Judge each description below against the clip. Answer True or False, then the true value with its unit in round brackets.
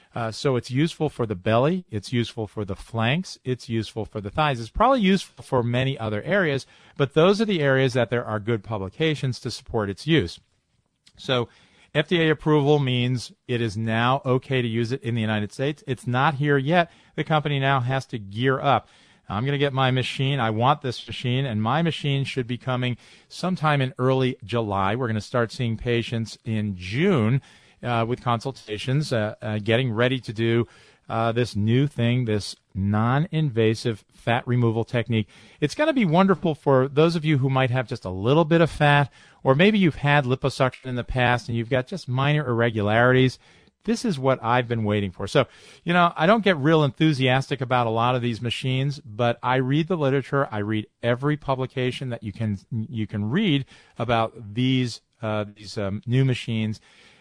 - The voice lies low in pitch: True (125 Hz)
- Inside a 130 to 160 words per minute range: False (195 wpm)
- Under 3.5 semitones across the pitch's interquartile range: False (3.8 semitones)